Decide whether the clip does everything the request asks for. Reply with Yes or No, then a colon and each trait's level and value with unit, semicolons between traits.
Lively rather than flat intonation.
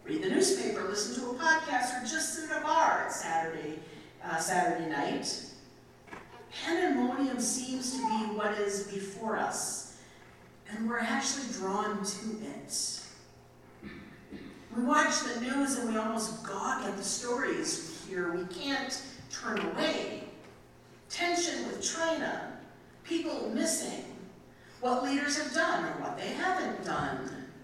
Yes: wide, 7.0 semitones